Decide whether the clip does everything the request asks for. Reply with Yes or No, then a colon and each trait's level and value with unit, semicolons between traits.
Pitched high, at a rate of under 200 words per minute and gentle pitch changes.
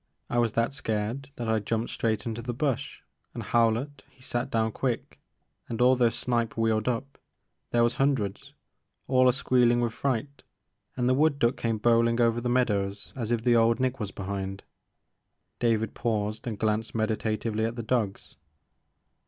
No: low, 115 Hz; average, 175 wpm; narrow, 2.2 semitones